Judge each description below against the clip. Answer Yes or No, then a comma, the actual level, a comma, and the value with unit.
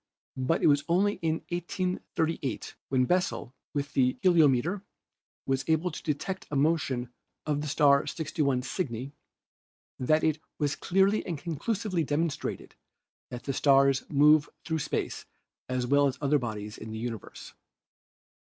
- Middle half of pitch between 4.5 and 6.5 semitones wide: No, average, 3.7 semitones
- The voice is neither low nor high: Yes, medium, 145 Hz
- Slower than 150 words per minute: Yes, average, 140 wpm